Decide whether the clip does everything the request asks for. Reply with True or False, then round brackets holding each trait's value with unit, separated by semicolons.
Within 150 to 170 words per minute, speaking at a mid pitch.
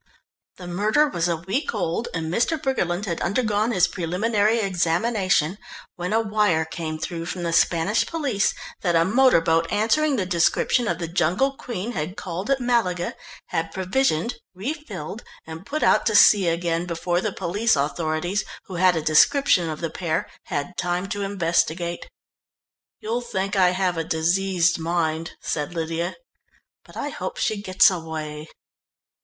True (160 wpm; 180 Hz)